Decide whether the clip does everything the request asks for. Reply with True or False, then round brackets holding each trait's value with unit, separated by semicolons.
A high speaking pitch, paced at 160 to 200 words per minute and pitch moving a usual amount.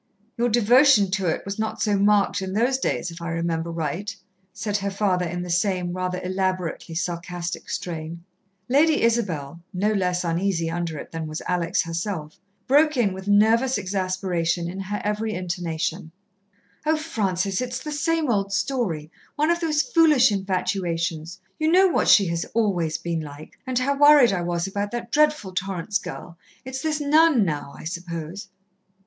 False (195 Hz; 170 wpm; 5.7 semitones)